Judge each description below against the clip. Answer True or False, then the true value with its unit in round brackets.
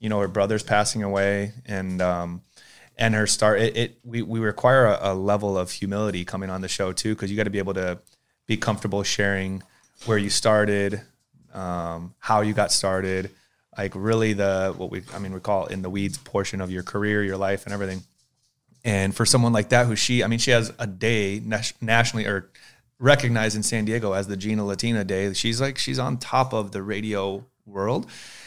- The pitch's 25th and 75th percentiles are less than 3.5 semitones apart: True (2.6 semitones)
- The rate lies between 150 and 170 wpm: False (205 wpm)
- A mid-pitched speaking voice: False (105 Hz)